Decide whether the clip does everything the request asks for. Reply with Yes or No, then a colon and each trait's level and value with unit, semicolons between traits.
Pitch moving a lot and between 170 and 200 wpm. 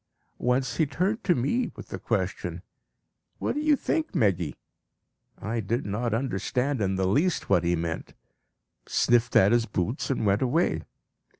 No: wide, 6.5 semitones; average, 160 wpm